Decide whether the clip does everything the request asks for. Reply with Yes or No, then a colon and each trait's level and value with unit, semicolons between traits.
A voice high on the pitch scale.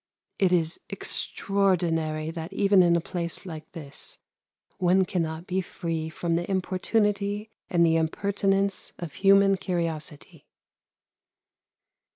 No: medium, 175 Hz